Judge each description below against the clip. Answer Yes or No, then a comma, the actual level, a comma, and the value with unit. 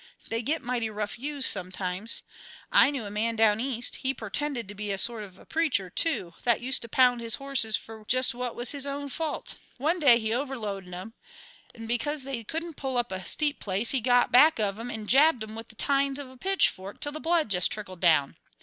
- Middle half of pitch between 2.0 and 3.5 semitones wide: No, average, 4.7 semitones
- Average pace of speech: No, fast, 225 wpm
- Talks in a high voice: Yes, high, 240 Hz